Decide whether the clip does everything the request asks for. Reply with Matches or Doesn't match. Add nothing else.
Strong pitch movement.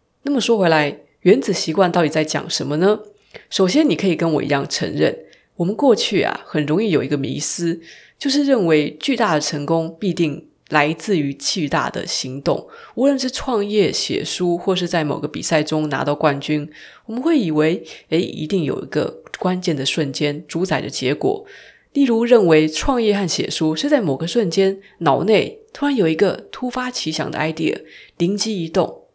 Matches